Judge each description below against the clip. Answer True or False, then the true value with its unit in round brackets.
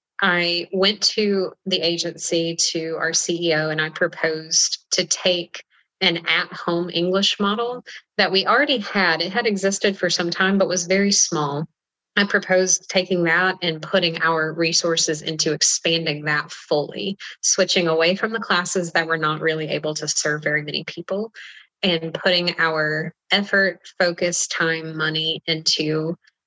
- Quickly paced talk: False (150 wpm)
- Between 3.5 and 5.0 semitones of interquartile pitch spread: False (2.8 semitones)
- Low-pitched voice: False (175 Hz)